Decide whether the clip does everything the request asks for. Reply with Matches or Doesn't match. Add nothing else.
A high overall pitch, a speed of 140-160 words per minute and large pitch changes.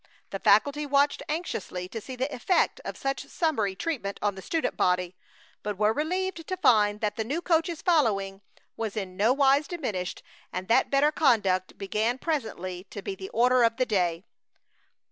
Doesn't match